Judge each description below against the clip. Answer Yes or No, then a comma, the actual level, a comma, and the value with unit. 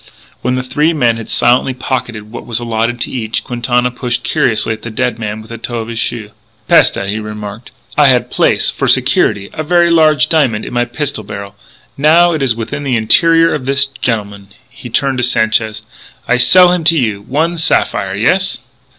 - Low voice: Yes, low, 120 Hz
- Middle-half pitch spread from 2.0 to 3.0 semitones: No, average, 4.7 semitones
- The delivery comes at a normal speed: Yes, average, 195 wpm